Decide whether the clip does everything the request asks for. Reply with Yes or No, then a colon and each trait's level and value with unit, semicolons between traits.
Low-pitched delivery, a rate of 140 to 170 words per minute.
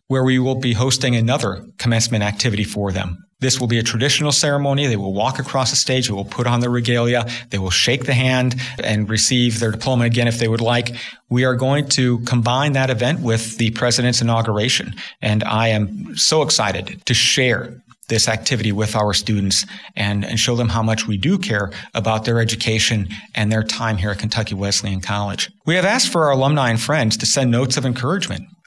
No: low, 120 Hz; fast, 205 wpm